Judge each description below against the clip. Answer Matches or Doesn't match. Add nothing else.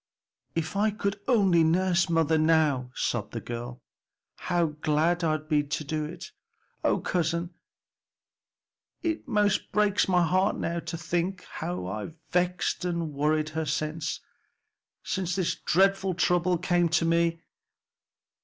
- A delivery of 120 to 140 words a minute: Matches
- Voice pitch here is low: Doesn't match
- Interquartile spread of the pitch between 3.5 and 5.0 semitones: Doesn't match